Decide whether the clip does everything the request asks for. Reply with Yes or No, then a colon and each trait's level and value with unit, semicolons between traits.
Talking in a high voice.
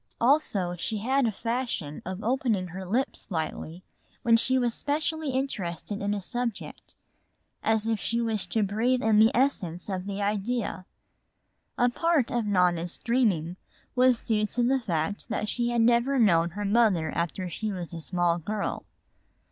Yes: high, 215 Hz